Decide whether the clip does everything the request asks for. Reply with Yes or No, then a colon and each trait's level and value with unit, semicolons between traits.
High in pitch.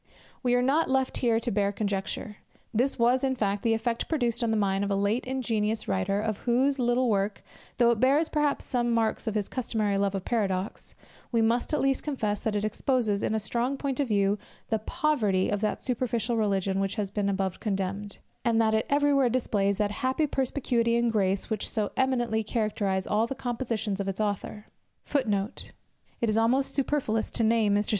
Yes: high, 225 Hz